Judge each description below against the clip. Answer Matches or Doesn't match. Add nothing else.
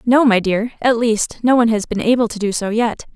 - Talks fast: Matches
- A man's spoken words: Doesn't match